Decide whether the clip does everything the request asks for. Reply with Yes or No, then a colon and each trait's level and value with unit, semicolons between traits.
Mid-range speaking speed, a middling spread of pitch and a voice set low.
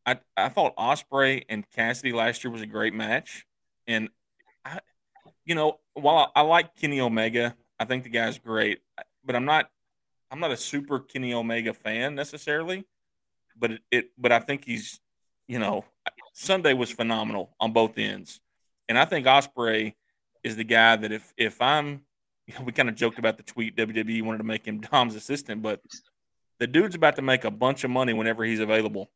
Yes: average, 185 wpm; average, 3.4 semitones; low, 120 Hz